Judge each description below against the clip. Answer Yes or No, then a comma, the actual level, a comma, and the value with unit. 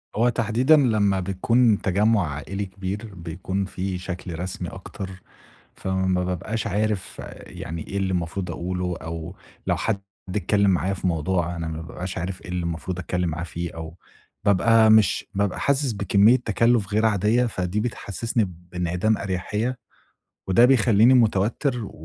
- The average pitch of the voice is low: Yes, very low, 95 Hz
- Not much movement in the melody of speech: No, average, 3.4 semitones